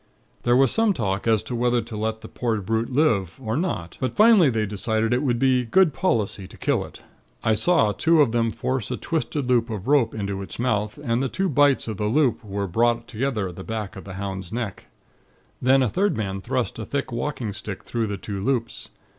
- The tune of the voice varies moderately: Yes, average, 4.0 semitones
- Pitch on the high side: No, low, 115 Hz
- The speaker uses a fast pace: Yes, fast, 220 wpm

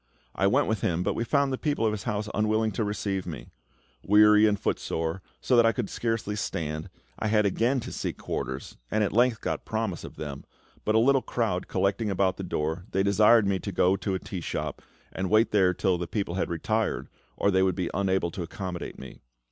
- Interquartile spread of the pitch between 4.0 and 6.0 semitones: No, average, 3.1 semitones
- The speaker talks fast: Yes, fast, 220 wpm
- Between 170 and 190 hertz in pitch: No, low, 100 Hz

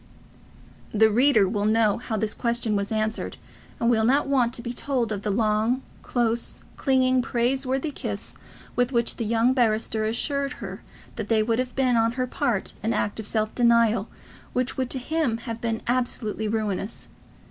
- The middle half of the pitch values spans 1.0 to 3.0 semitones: Yes, narrow, 2.6 semitones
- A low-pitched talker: No, high, 235 Hz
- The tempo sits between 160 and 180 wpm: Yes, average, 170 wpm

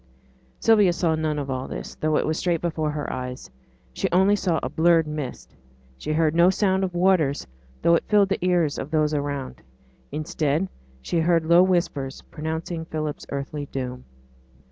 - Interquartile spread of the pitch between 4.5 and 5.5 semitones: No, average, 3.1 semitones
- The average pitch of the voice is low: No, medium, 160 Hz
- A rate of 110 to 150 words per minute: No, average, 170 wpm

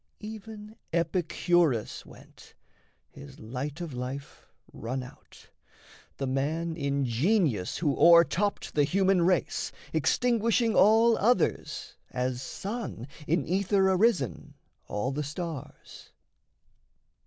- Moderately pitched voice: Yes, medium, 165 Hz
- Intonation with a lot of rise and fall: Yes, wide, 6.6 semitones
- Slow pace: Yes, slow, 105 wpm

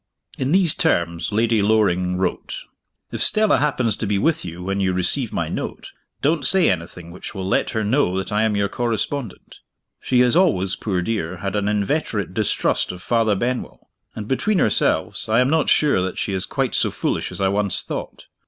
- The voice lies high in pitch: No, low, 105 Hz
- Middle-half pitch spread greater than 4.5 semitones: Yes, average, 5.2 semitones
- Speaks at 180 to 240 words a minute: Yes, average, 195 wpm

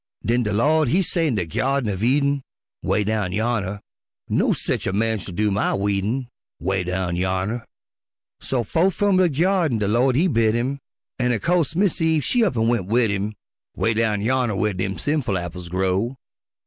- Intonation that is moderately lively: No, wide, 5.9 semitones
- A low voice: Yes, low, 115 Hz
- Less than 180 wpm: No, average, 190 wpm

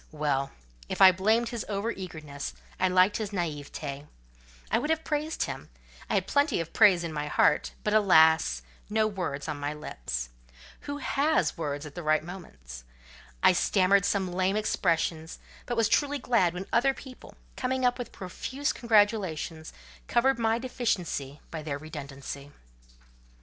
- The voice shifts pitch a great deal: Yes, wide, 7.0 semitones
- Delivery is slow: No, average, 155 wpm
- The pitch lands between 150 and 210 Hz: Yes, medium, 185 Hz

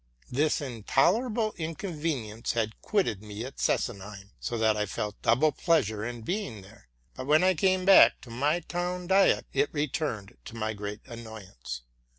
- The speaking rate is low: No, average, 160 wpm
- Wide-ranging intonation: Yes, wide, 7.7 semitones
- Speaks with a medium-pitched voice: No, low, 120 Hz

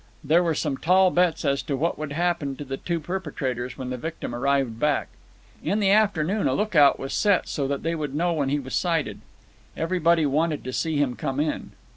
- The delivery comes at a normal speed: No, fast, 210 wpm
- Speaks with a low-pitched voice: No, medium, 155 Hz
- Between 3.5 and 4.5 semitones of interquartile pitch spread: Yes, average, 3.8 semitones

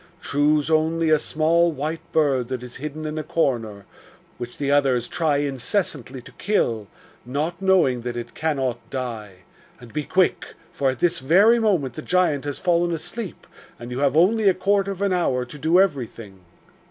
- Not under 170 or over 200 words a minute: Yes, average, 175 wpm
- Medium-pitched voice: Yes, medium, 150 Hz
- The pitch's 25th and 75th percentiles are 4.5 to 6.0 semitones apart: Yes, average, 5.2 semitones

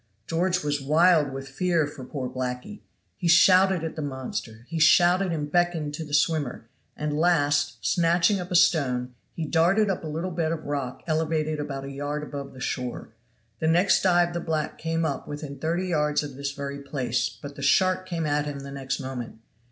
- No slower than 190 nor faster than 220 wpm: Yes, average, 195 wpm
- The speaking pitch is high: No, medium, 150 Hz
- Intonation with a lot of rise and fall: No, average, 3.5 semitones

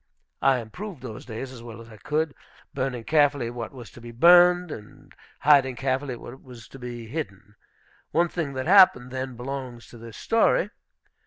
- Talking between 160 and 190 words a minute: Yes, average, 175 wpm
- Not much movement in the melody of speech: No, average, 4.0 semitones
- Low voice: Yes, low, 130 Hz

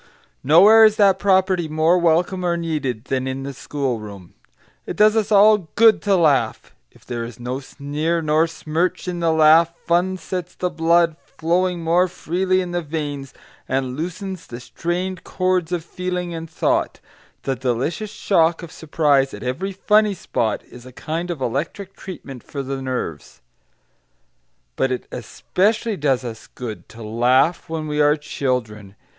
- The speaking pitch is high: No, medium, 160 Hz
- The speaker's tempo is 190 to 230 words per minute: No, average, 160 wpm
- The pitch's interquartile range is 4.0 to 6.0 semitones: Yes, wide, 5.4 semitones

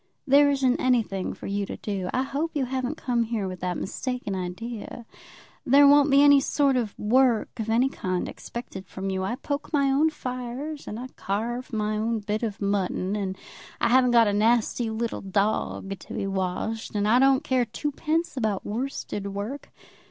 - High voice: Yes, high, 235 Hz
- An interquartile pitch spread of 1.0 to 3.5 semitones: No, average, 4.8 semitones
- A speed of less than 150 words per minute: No, average, 185 wpm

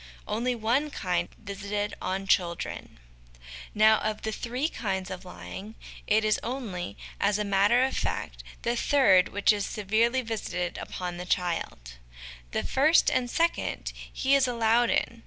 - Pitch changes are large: No, average, 4.1 semitones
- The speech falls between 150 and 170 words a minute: Yes, average, 155 wpm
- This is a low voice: No, high, 215 Hz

